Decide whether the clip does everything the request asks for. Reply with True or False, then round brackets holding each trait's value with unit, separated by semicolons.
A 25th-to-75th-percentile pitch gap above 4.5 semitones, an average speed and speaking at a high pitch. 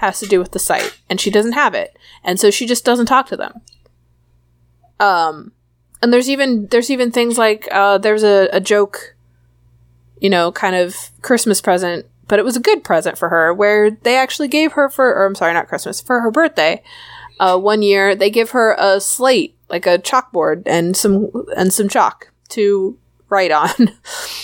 True (5.4 semitones; 195 wpm; 205 Hz)